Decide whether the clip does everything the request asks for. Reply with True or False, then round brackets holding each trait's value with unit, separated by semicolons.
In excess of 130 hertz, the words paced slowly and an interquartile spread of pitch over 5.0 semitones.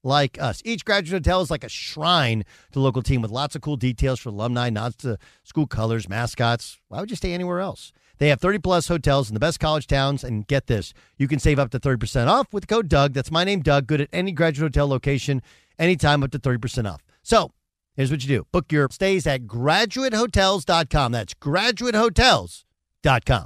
False (140 Hz; 205 wpm; 5.6 semitones)